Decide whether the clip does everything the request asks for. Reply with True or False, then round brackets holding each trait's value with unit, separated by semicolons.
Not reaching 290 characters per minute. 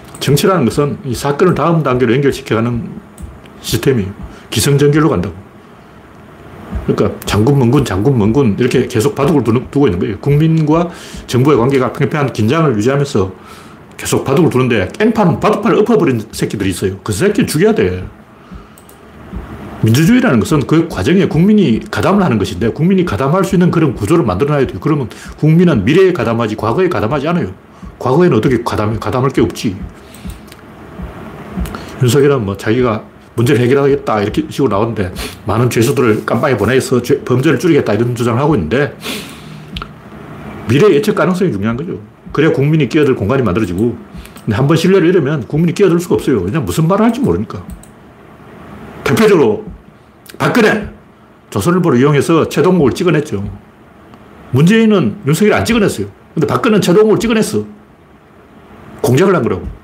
False (375 characters per minute)